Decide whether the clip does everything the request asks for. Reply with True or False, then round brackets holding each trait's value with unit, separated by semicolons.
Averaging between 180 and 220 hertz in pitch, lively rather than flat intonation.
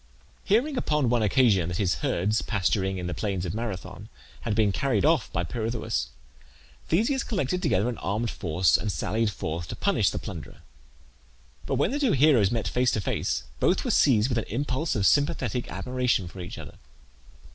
False (115 Hz; 5.9 semitones)